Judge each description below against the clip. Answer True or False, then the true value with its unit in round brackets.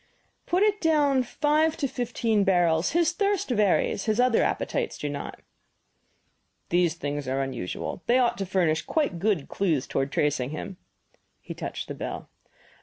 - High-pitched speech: True (200 Hz)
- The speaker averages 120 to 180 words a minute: True (155 wpm)